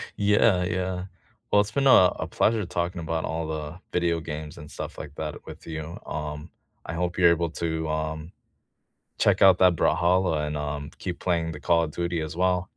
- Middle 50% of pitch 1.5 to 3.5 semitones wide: Yes, narrow, 2.6 semitones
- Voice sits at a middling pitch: No, very low, 85 Hz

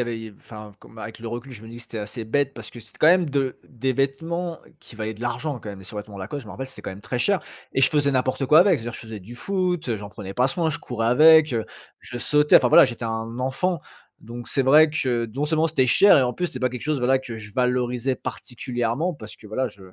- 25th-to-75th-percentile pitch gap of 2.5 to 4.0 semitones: No, average, 4.4 semitones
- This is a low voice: Yes, low, 125 Hz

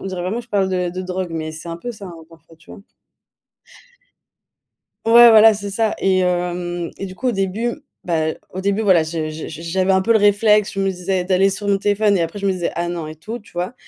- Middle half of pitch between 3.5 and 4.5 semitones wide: No, average, 2.8 semitones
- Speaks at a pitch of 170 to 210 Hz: Yes, high, 190 Hz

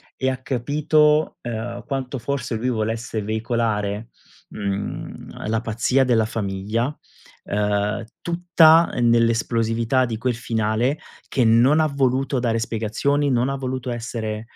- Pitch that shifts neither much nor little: Yes, average, 3.0 semitones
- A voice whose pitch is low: Yes, low, 120 Hz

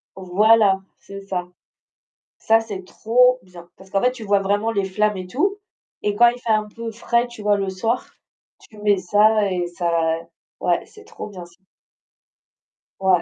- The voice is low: No, high, 205 Hz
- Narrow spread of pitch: No, average, 3.1 semitones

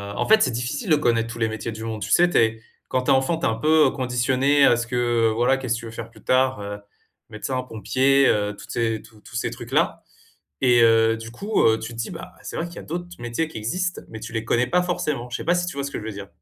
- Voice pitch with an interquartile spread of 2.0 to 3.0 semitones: No, average, 3.6 semitones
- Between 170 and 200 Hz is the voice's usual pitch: No, low, 120 Hz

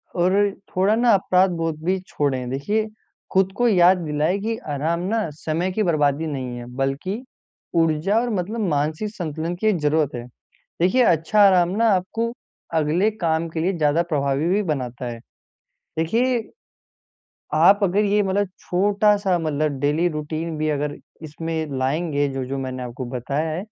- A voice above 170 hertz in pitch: No, medium, 165 Hz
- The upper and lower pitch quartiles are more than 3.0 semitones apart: Yes, average, 4.8 semitones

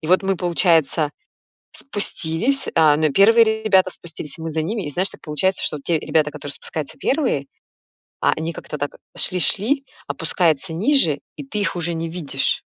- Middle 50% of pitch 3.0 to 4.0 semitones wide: No, average, 4.4 semitones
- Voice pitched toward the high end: No, medium, 170 Hz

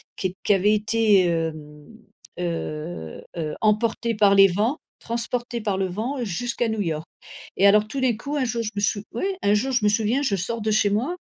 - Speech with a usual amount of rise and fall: Yes, average, 3.9 semitones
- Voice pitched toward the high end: Yes, high, 210 Hz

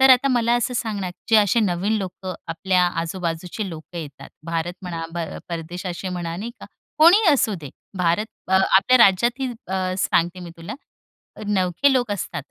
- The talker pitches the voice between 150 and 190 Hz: Yes, medium, 185 Hz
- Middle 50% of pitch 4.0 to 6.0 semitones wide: Yes, average, 4.7 semitones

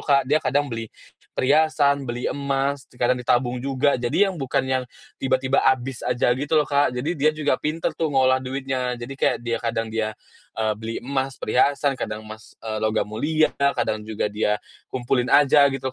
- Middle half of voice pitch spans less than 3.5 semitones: Yes, average, 2.9 semitones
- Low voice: Yes, low, 130 Hz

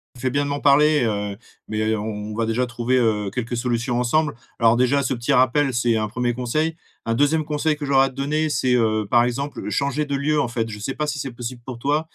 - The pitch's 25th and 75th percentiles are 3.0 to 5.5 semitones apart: Yes, average, 3.5 semitones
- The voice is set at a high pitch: No, low, 125 Hz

